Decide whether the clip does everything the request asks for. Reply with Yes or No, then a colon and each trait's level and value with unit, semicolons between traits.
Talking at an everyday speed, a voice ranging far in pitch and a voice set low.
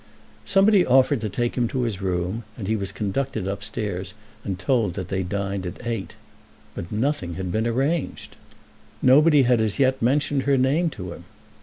Yes: average, 175 wpm; wide, 5.7 semitones; low, 110 Hz